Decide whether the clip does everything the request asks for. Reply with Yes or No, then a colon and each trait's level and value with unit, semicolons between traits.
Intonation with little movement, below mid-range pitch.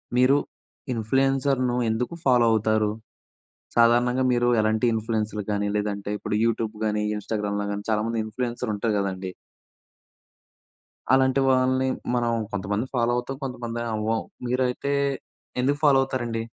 No: average, 3.0 semitones; low, 115 Hz